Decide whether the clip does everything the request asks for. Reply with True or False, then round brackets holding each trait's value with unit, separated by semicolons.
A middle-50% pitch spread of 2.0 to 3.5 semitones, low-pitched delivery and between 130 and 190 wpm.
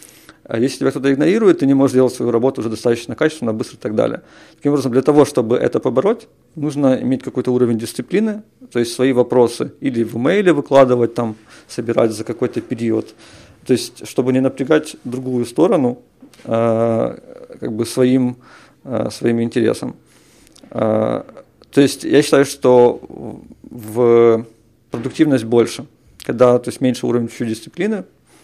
True (2.9 semitones; 125 Hz; 150 wpm)